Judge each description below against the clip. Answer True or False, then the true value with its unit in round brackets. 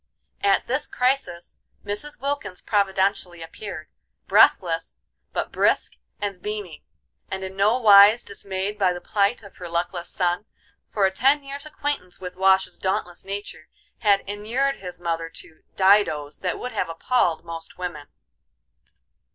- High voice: True (195 Hz)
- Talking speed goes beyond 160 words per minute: False (140 wpm)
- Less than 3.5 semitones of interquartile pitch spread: True (3.1 semitones)